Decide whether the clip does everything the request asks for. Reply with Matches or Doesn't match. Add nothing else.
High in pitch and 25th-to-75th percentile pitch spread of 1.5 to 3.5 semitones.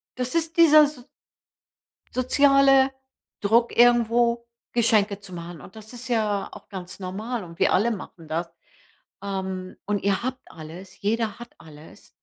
Doesn't match